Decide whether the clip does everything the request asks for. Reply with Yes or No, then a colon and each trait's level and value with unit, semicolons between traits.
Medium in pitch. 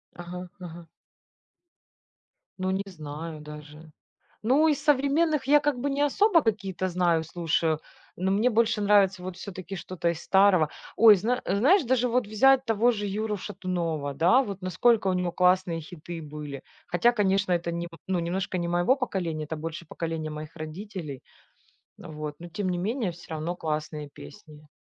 Yes: medium, 180 Hz